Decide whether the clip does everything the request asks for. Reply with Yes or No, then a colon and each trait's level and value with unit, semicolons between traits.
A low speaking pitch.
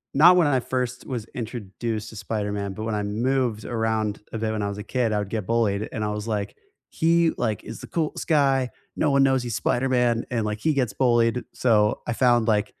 Yes: low, 115 Hz